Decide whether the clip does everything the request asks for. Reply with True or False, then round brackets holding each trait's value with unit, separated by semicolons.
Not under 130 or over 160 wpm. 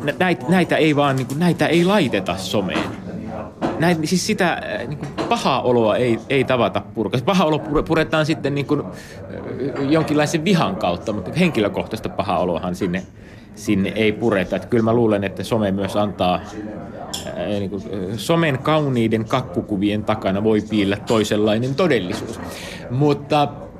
True (140 wpm)